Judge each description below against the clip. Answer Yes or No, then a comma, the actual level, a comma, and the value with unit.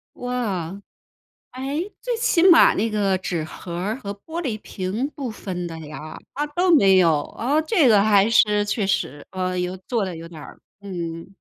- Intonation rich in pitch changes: Yes, wide, 5.9 semitones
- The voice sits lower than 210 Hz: Yes, high, 200 Hz